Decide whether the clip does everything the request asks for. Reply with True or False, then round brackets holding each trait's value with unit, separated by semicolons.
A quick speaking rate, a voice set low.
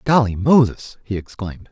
False (140 wpm; 115 Hz)